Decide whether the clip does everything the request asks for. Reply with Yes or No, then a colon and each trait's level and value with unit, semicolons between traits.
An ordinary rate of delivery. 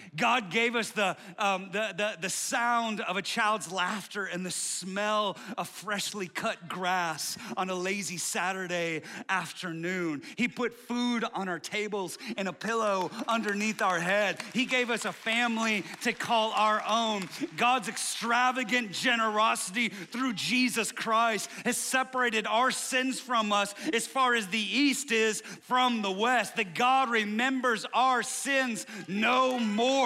Yes: average, 150 wpm